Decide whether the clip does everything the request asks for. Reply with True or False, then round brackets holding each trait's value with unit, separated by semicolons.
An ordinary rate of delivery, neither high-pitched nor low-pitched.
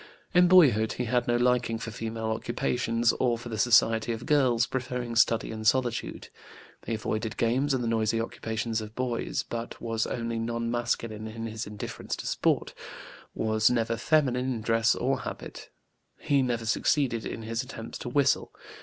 False (170 wpm; 115 Hz)